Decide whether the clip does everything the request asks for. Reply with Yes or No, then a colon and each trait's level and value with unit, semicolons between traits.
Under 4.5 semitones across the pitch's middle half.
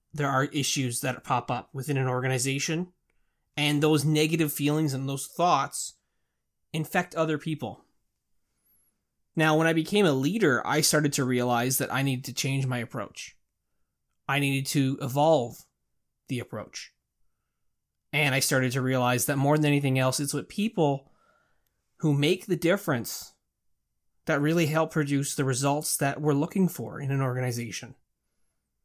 Yes: average, 3.2 semitones